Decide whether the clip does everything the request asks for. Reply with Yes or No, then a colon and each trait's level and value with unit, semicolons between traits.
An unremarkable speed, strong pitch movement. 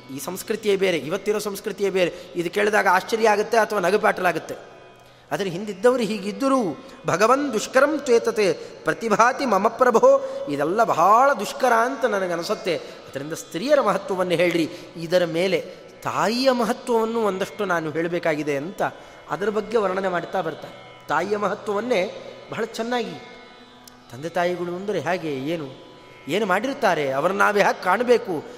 No: fast, 120 wpm; wide, 5.9 semitones